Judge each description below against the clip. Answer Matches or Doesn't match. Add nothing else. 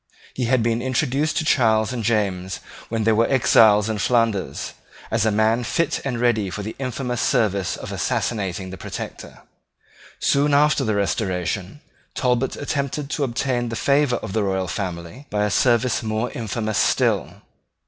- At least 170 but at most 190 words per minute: Doesn't match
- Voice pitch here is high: Doesn't match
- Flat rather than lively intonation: Doesn't match